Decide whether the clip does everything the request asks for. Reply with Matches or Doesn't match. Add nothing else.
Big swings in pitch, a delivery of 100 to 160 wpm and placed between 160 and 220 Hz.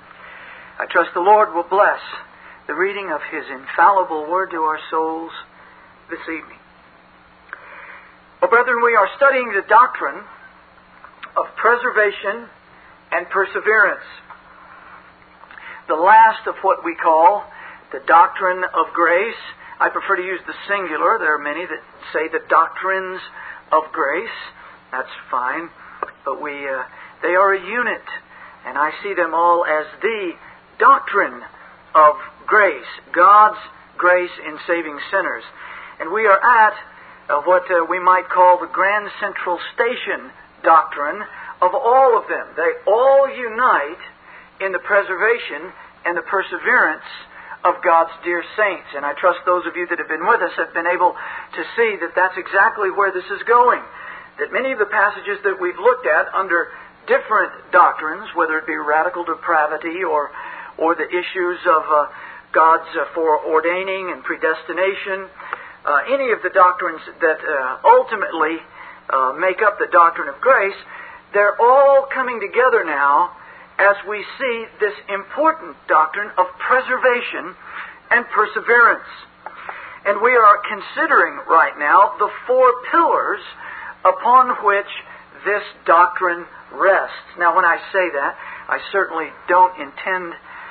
Matches